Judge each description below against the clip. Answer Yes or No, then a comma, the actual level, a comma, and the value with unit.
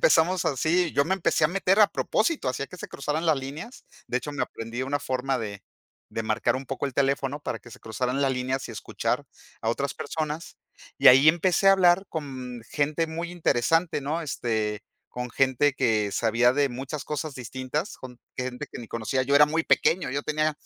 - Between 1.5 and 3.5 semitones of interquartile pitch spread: No, average, 4.1 semitones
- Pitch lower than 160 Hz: Yes, medium, 140 Hz